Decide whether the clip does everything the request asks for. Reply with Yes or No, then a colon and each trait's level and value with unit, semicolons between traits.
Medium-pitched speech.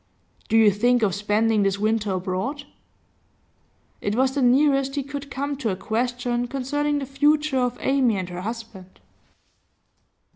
No: high, 245 Hz